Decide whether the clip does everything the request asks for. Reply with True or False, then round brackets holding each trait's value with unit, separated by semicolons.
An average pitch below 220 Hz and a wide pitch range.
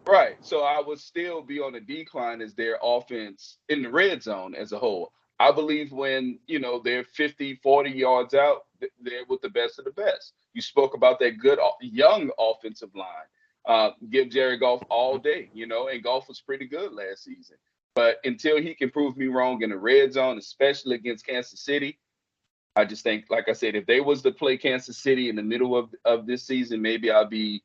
True (135 Hz; 8.9 semitones)